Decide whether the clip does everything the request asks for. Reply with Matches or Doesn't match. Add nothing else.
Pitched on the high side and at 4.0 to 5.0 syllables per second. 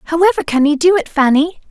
Doesn't match